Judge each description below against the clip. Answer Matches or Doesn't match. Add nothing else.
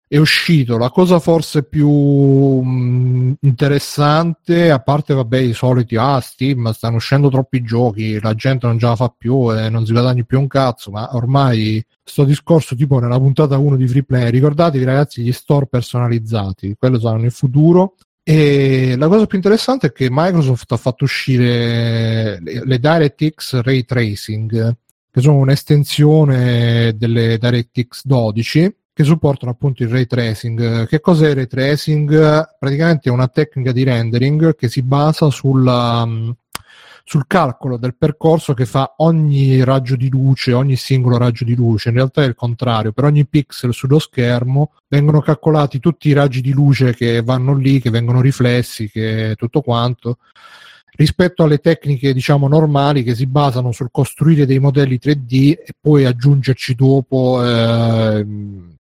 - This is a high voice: Doesn't match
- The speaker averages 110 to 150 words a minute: Doesn't match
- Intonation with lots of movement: Doesn't match